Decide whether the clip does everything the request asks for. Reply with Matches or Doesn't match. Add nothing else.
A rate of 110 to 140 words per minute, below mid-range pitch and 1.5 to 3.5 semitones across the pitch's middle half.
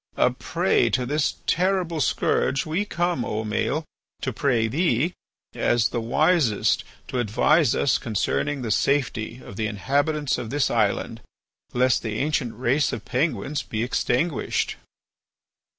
Doesn't match